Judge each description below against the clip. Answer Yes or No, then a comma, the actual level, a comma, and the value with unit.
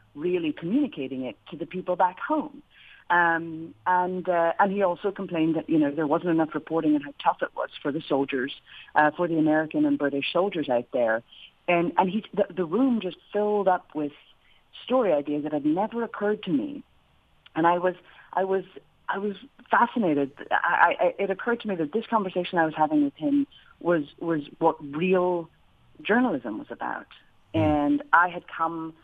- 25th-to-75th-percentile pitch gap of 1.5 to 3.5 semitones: No, average, 4.8 semitones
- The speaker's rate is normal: Yes, average, 185 wpm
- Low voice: No, medium, 175 Hz